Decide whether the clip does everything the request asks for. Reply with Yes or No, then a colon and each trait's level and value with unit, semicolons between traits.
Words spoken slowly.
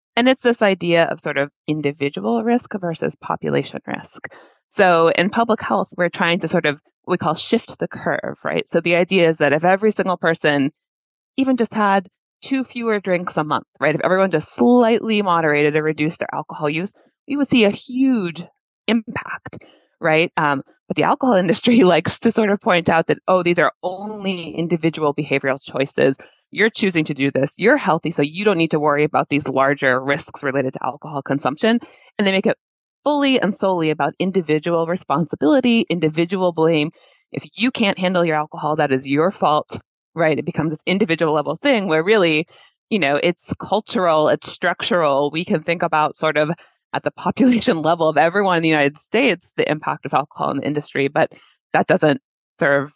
No: average, 190 wpm